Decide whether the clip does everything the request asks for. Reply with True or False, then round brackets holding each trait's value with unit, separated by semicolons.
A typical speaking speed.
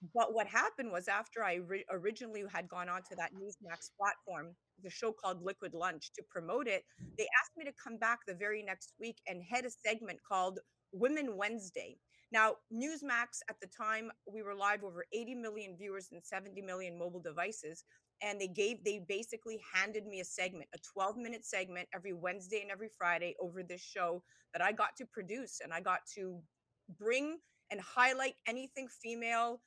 True (185 wpm)